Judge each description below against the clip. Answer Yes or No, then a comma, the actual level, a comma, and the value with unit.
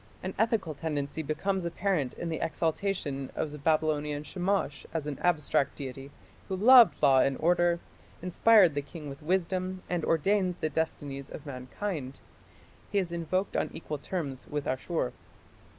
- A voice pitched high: No, medium, 160 Hz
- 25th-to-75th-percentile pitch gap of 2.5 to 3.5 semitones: No, average, 4.3 semitones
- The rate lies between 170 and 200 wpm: No, average, 150 wpm